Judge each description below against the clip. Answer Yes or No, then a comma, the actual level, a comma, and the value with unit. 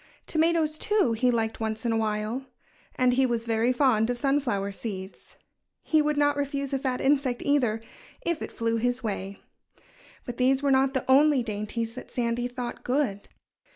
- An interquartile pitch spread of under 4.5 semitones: Yes, average, 3.6 semitones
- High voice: Yes, high, 245 Hz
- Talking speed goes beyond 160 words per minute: Yes, average, 175 wpm